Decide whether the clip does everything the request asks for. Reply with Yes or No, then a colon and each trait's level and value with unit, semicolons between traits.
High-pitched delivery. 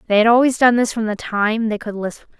Yes: high, 220 Hz